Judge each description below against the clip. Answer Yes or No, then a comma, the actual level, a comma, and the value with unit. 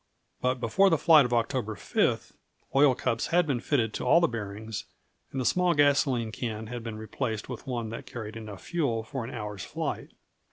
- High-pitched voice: No, low, 120 Hz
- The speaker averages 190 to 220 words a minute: Yes, average, 195 wpm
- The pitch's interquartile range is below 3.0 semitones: No, average, 4.3 semitones